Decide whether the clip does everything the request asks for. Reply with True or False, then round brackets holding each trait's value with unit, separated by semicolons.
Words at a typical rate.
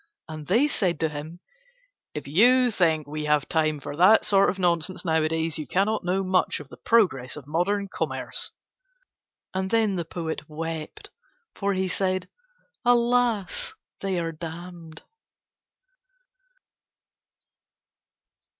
False (125 wpm)